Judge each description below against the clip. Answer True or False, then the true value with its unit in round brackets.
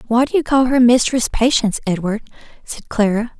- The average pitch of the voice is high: True (235 Hz)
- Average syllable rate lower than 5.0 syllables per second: False (5.6 syllables/s)